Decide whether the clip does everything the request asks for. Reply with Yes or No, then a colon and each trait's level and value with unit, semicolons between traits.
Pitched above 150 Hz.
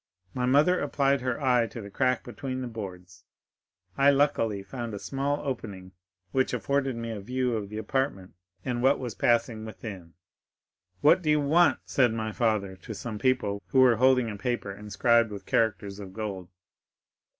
No: low, 115 Hz